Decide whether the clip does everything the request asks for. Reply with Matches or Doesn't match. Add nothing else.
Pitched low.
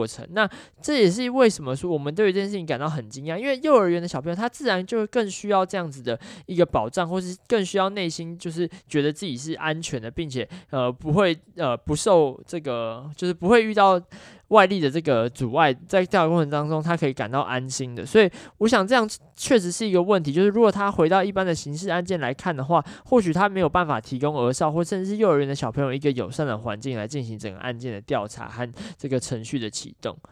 Doesn't match